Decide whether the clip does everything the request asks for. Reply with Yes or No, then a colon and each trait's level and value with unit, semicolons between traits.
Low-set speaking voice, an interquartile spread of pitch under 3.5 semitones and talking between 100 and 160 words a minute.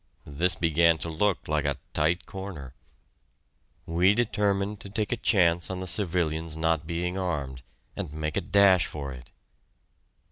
No: very low, 85 Hz; average, 3.8 semitones; average, 150 wpm